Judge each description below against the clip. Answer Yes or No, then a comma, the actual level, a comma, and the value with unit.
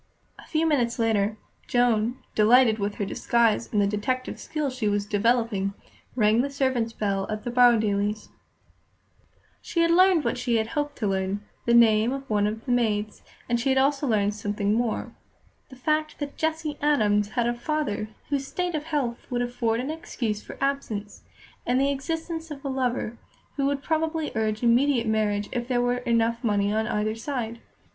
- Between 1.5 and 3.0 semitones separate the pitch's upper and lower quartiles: No, average, 4.4 semitones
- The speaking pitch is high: Yes, high, 235 Hz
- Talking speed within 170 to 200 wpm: Yes, average, 180 wpm